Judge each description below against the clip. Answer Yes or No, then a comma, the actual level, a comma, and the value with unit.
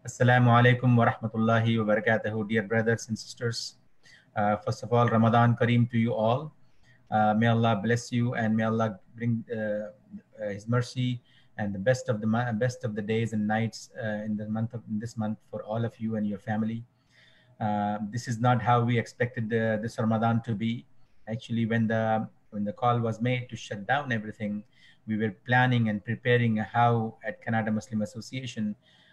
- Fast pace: No, average, 185 wpm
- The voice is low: Yes, low, 115 Hz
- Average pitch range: No, narrow, 1.9 semitones